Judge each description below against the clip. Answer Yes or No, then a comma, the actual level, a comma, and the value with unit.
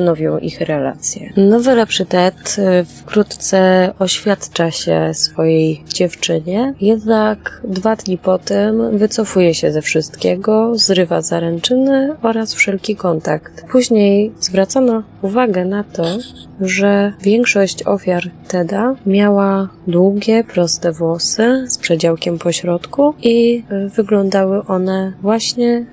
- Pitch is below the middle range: No, high, 195 Hz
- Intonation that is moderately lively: Yes, average, 4.0 semitones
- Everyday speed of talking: No, slow, 105 wpm